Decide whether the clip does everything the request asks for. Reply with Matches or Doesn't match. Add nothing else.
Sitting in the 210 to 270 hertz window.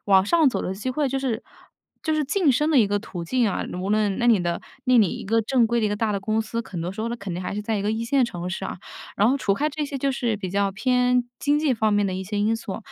Matches